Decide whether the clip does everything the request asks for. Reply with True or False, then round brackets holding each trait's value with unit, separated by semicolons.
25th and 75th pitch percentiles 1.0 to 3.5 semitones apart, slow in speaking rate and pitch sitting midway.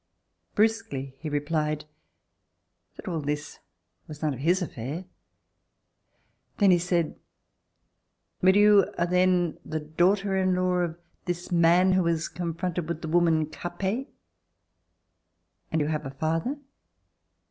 True (2.9 semitones; 125 wpm; 170 Hz)